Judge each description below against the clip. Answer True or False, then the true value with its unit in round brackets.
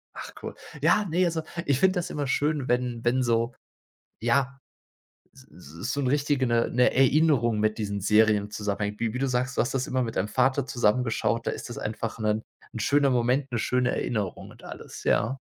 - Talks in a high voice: False (125 Hz)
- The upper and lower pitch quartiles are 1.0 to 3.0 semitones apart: False (3.7 semitones)